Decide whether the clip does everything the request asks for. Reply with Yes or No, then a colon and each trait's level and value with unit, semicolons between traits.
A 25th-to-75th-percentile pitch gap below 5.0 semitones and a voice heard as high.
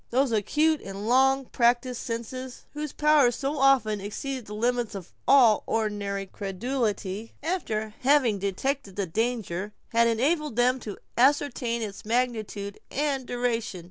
Yes: average, 4.2 semitones; high, 235 Hz